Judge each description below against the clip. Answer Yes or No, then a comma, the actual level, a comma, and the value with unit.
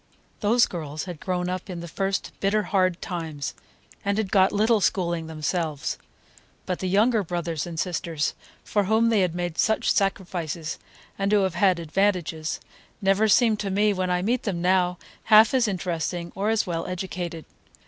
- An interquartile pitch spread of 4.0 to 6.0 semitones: No, average, 3.1 semitones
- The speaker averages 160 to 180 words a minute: Yes, average, 170 wpm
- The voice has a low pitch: No, medium, 185 Hz